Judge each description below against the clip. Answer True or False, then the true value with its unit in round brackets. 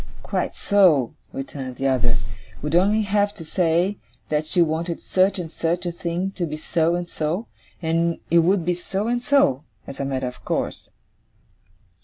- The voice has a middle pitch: True (170 Hz)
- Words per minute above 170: True (180 wpm)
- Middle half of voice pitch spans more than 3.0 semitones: True (3.7 semitones)